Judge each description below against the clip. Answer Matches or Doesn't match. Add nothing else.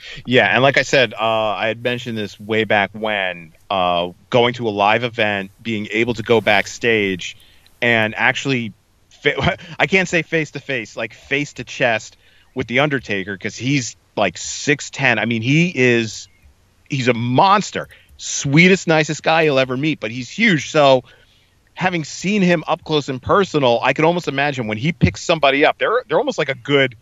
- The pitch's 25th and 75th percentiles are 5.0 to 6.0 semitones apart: Matches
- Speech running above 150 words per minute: Matches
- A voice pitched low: Matches